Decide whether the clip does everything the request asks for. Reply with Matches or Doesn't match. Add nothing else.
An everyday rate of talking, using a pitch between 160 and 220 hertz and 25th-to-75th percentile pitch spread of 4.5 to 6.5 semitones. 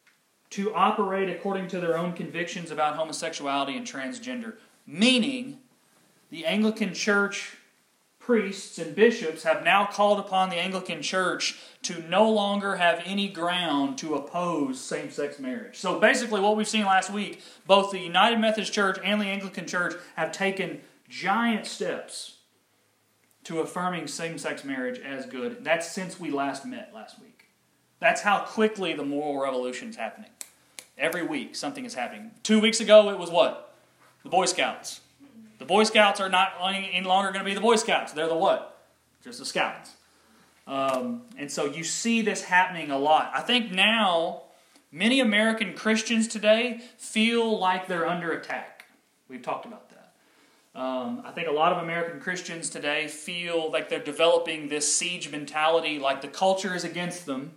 Matches